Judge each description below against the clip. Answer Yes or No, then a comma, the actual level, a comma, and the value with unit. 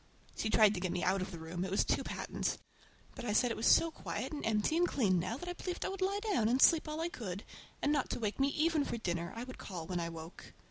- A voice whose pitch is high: Yes, high, 225 Hz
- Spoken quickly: Yes, fast, 280 wpm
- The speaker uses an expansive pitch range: Yes, wide, 8.9 semitones